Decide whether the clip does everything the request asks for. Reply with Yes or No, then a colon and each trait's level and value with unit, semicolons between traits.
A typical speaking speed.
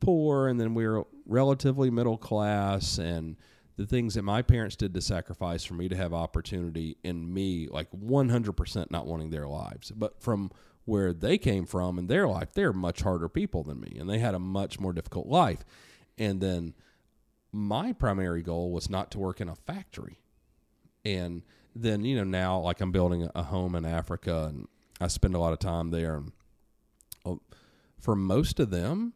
Yes: average, 190 wpm